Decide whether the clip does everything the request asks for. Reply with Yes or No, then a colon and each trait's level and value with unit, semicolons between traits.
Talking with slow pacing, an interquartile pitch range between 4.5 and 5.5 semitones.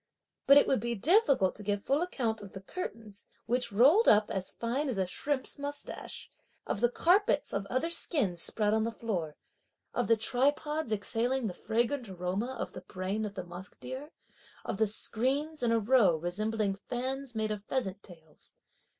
No: average, 185 wpm; average, 5.0 semitones